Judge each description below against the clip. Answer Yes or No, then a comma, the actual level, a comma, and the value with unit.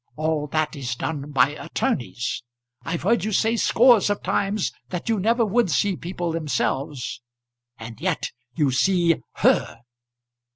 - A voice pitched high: No, medium, 165 Hz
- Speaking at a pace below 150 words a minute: Yes, average, 140 wpm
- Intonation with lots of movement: Yes, wide, 6.3 semitones